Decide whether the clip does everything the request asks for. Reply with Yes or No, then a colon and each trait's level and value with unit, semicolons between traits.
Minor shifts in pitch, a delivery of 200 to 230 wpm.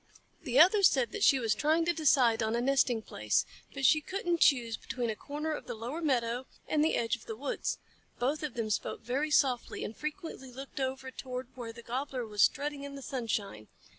No: average, 3.9 semitones; fast, 205 wpm